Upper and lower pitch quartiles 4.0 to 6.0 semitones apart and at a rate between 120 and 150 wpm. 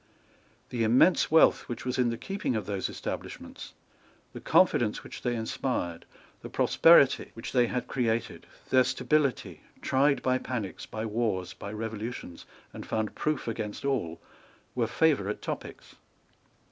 No: average, 3.4 semitones; average, 140 wpm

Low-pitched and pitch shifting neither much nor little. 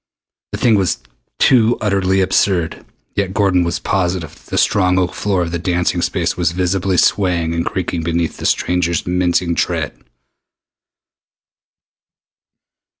No: very low, 90 Hz; narrow, 1.9 semitones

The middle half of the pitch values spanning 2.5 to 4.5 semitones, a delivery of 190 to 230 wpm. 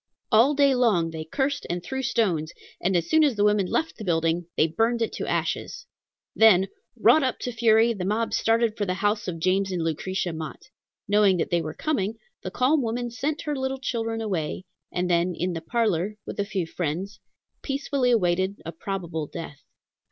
No: wide, 5.4 semitones; average, 195 wpm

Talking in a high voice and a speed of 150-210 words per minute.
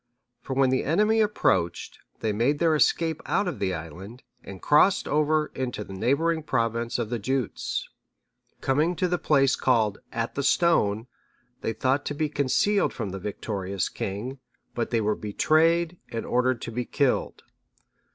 No: low, 130 Hz; average, 160 wpm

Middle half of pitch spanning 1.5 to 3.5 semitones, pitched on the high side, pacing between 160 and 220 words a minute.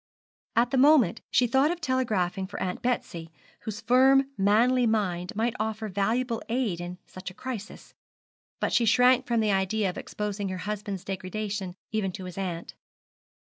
No: average, 4.5 semitones; high, 215 Hz; average, 165 wpm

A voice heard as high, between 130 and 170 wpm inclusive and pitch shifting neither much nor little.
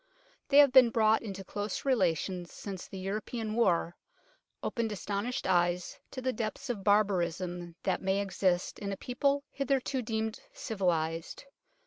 Yes: high, 205 Hz; average, 145 wpm; average, 4.6 semitones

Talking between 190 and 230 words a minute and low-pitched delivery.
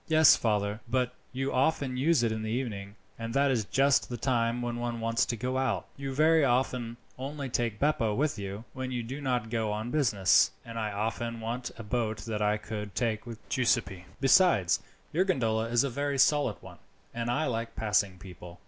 Yes: average, 200 wpm; low, 120 Hz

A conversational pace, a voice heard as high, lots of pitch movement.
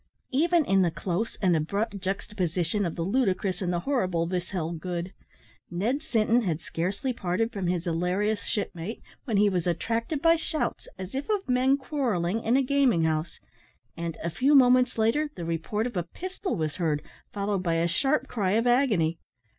Yes: average, 180 wpm; high, 200 Hz; wide, 6.4 semitones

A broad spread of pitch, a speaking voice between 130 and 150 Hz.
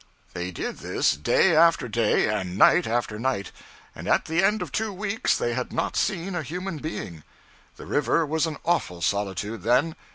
Yes: wide, 8.6 semitones; medium, 140 Hz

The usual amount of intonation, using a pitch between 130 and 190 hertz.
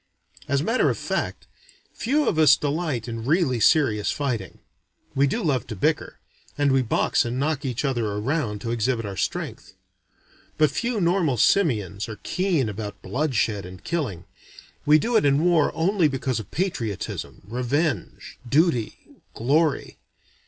No: wide, 5.9 semitones; low, 135 Hz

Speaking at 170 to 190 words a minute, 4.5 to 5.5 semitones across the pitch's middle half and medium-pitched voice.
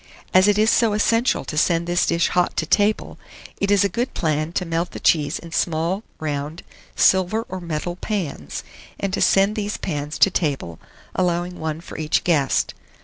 No: average, 185 wpm; average, 4.0 semitones; medium, 175 Hz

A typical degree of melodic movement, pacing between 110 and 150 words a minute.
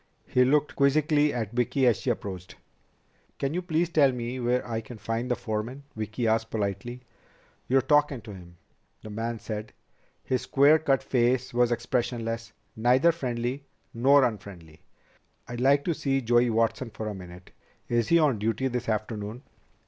No: average, 3.4 semitones; average, 165 wpm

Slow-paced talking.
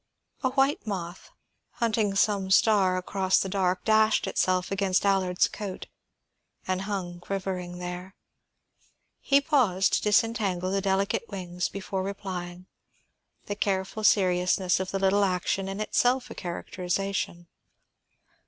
Yes: slow, 125 wpm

